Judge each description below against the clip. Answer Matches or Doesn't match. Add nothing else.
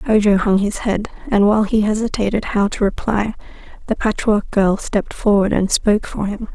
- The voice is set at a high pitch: Matches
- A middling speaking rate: Matches